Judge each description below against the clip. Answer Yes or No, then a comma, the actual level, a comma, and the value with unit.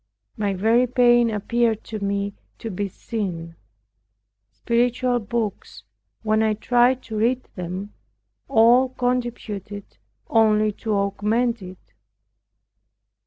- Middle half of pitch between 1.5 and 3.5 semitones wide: Yes, average, 3.1 semitones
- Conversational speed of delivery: No, slow, 105 wpm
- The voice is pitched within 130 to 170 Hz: No, high, 220 Hz